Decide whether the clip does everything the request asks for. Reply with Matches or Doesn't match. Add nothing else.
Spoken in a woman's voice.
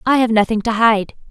Matches